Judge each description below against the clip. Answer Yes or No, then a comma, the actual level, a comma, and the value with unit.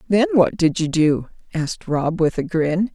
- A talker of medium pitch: Yes, medium, 180 Hz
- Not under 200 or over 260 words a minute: Yes, fast, 205 wpm